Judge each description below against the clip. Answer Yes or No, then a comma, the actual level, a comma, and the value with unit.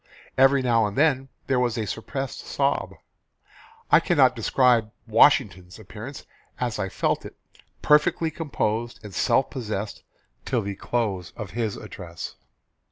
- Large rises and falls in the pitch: No, average, 4.3 semitones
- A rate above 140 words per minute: No, slow, 135 wpm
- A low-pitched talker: Yes, low, 115 Hz